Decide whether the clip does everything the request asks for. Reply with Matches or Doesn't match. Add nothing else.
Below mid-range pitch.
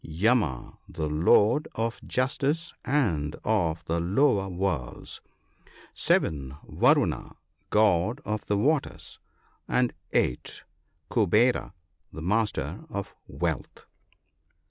Matches